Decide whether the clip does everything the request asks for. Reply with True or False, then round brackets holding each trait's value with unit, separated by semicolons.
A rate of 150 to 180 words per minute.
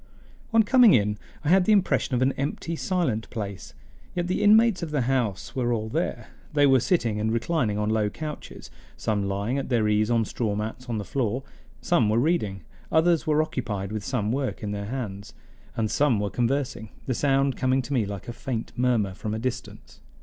False (200 wpm)